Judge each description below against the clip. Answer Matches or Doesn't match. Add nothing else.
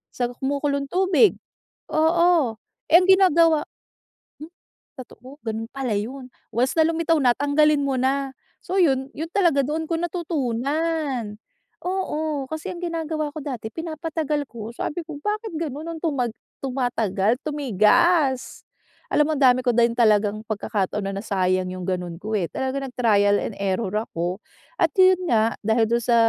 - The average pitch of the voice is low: Doesn't match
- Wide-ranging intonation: Matches